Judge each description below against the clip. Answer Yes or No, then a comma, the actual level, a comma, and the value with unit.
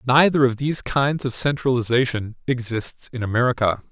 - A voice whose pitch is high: No, low, 125 Hz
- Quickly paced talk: No, average, 140 wpm